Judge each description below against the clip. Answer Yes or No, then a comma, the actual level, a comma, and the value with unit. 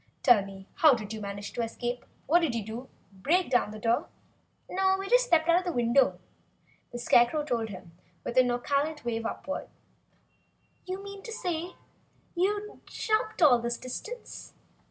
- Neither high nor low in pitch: No, very high, 250 Hz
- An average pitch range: No, wide, 7.3 semitones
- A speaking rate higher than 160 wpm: No, average, 155 wpm